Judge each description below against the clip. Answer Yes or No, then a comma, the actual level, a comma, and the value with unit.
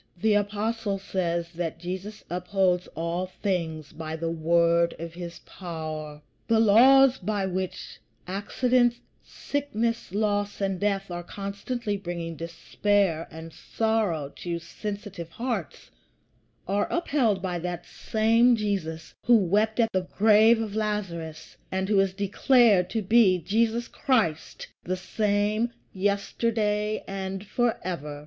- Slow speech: Yes, slow, 125 wpm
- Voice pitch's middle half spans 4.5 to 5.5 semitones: No, average, 4.1 semitones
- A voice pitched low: No, high, 195 Hz